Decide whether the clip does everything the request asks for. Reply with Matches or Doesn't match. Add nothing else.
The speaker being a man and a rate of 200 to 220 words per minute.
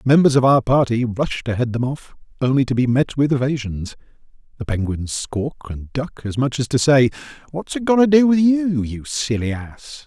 Matches